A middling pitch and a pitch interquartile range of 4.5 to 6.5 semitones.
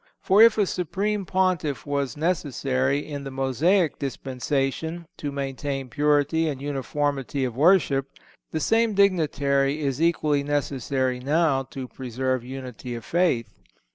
No: medium, 145 Hz; average, 3.6 semitones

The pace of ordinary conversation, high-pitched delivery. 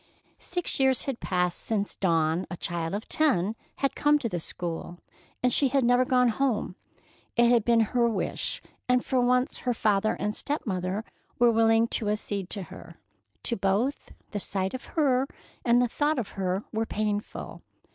Yes: average, 175 wpm; high, 225 Hz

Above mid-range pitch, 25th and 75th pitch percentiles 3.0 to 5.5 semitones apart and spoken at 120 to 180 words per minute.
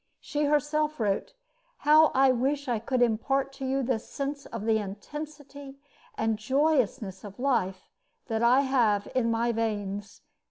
Yes: very high, 255 Hz; average, 4.4 semitones; average, 150 wpm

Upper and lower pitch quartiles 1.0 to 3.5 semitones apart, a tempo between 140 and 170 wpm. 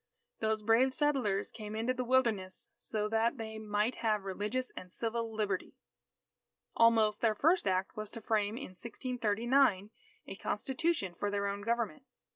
Yes: average, 2.7 semitones; average, 150 wpm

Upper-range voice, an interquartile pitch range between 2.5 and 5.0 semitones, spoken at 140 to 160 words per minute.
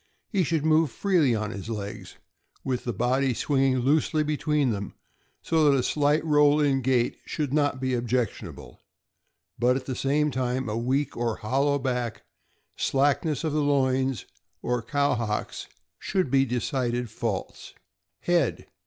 No: low, 135 Hz; average, 3.3 semitones; average, 155 wpm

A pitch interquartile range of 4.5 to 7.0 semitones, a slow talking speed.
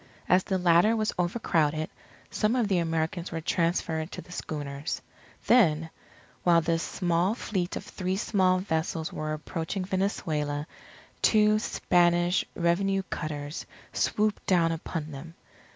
No: average, 3.2 semitones; slow, 130 wpm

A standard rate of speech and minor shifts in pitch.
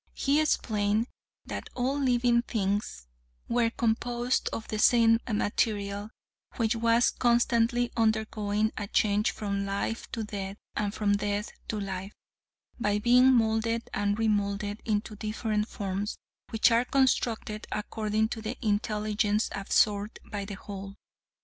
No: slow, 130 wpm; narrow, 2.2 semitones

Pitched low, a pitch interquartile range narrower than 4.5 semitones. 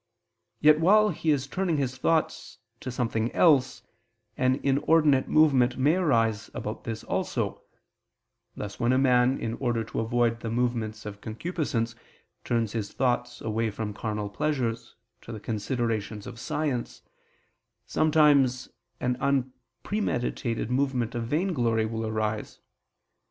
Yes: low, 125 Hz; average, 3.6 semitones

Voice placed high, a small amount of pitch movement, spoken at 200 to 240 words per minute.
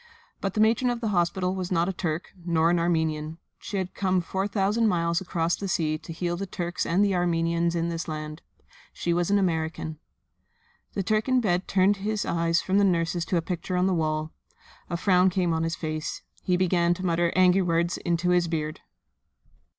No: medium, 175 Hz; narrow, 2.2 semitones; fast, 205 wpm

